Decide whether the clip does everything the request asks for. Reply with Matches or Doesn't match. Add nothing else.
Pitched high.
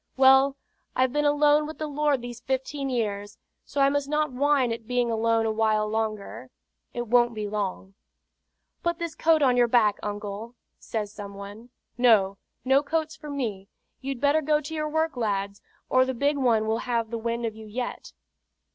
Matches